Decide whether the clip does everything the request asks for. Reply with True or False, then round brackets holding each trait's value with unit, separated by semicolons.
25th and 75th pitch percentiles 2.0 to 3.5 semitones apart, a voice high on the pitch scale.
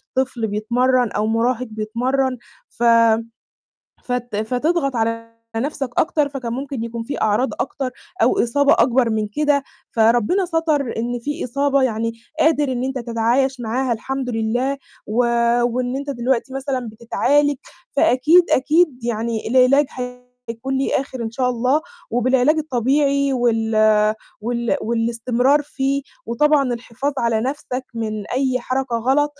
True (3.0 semitones; 255 Hz)